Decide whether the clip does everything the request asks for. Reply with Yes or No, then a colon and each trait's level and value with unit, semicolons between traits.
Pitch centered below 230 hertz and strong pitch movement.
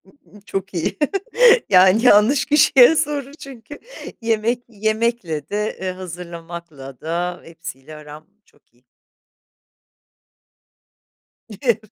Yes: high, 200 Hz; wide, 6.0 semitones